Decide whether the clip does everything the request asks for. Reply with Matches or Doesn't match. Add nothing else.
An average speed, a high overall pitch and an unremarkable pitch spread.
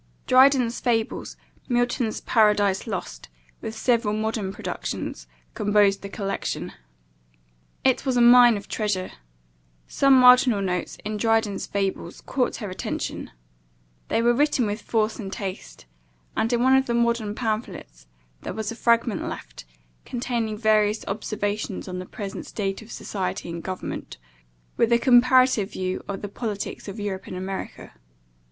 Matches